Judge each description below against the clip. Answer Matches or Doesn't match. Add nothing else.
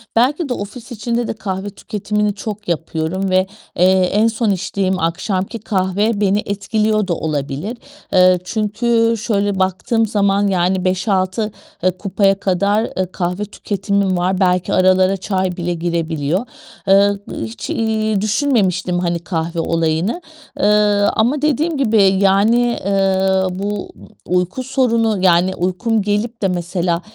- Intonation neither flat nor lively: Matches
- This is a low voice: Doesn't match